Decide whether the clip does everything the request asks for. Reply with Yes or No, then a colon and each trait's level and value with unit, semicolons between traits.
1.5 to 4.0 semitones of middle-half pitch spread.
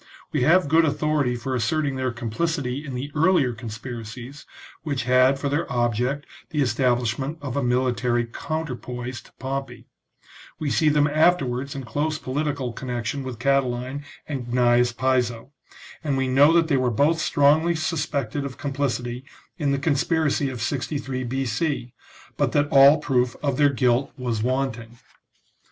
Yes: average, 2.9 semitones